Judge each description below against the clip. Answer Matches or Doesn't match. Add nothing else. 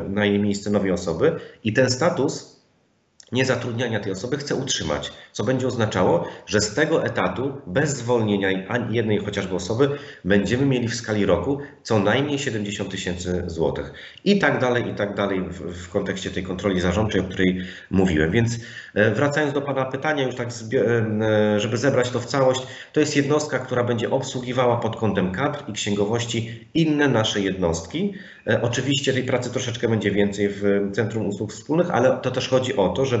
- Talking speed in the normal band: Doesn't match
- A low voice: Matches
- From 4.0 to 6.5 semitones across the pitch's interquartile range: Matches